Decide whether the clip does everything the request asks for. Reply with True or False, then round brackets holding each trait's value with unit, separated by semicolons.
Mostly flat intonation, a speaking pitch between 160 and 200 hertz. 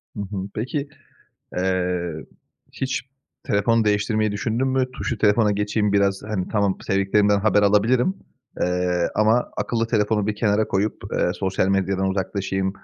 False (2.2 semitones; 105 Hz)